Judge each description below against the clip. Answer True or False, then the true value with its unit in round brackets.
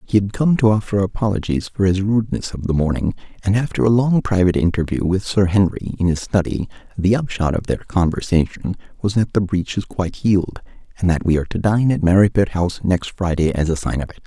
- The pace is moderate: False (220 wpm)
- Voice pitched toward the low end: True (95 Hz)